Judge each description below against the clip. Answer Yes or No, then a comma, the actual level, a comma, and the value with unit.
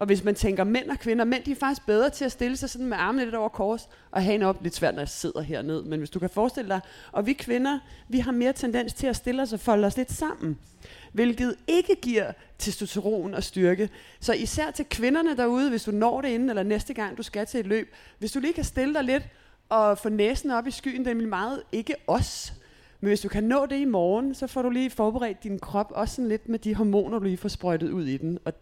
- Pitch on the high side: Yes, high, 225 Hz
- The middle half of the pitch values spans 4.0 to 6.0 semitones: Yes, average, 4.4 semitones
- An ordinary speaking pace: No, fast, 260 wpm